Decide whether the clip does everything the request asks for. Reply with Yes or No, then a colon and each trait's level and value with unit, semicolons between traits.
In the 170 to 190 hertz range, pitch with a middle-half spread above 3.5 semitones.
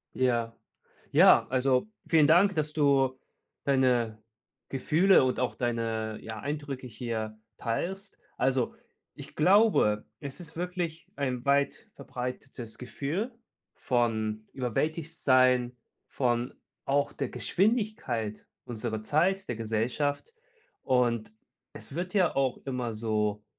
No: low, 130 Hz; average, 4.8 semitones